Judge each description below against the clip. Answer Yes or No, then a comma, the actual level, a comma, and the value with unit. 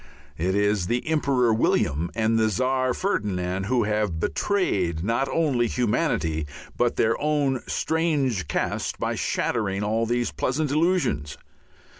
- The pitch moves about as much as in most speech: No, wide, 5.7 semitones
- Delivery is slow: Yes, slow, 130 wpm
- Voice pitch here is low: Yes, low, 115 Hz